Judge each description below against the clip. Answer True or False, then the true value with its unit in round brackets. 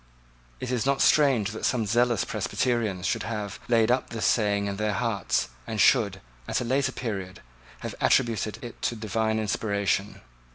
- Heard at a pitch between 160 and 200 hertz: False (110 Hz)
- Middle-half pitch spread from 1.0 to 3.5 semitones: True (2.8 semitones)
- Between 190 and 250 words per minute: False (165 wpm)